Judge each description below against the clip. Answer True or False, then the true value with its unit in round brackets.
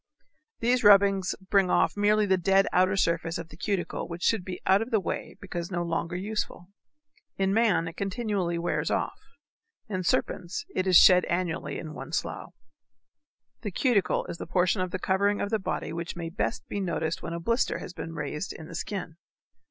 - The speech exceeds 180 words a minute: True (190 wpm)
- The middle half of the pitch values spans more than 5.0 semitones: False (3.0 semitones)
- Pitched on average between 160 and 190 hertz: True (185 Hz)